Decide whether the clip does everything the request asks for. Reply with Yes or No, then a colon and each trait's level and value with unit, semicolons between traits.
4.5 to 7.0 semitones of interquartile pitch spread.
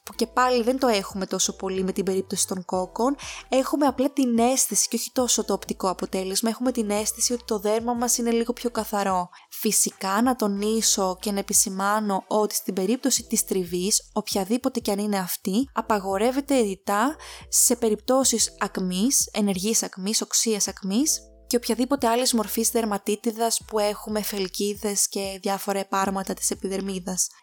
No: average, 3.3 semitones